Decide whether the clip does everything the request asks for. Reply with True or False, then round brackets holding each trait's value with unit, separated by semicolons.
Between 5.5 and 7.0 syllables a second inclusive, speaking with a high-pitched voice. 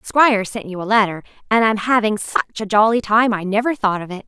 True (5.6 syllables/s; 215 Hz)